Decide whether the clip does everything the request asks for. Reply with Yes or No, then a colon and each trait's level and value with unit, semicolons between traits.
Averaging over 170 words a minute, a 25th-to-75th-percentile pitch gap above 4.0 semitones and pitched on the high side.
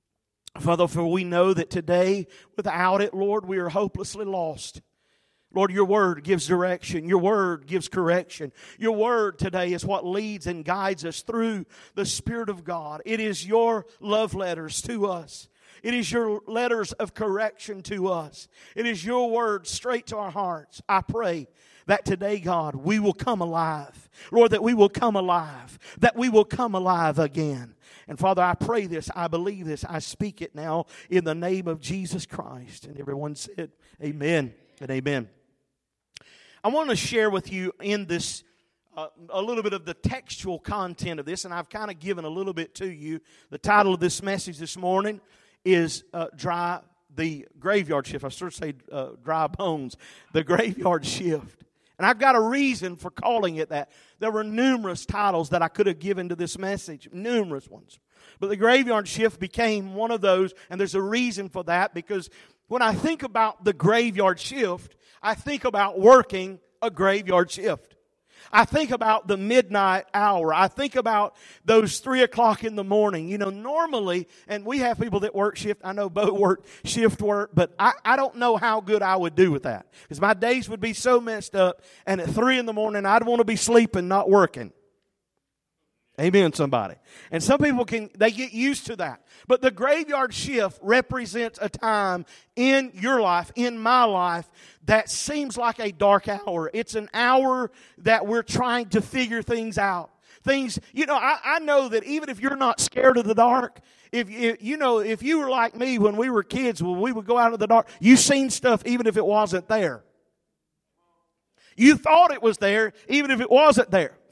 Yes: average, 195 wpm; average, 4.6 semitones; high, 200 Hz